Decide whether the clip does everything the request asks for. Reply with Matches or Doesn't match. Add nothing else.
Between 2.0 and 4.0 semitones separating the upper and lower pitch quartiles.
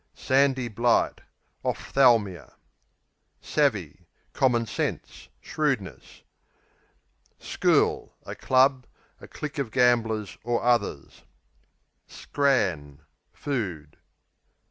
Doesn't match